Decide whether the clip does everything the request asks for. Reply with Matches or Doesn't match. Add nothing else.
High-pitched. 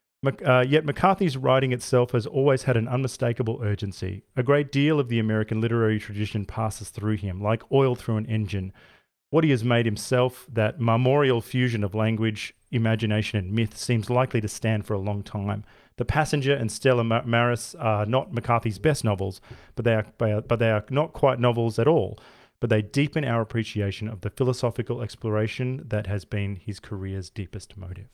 Doesn't match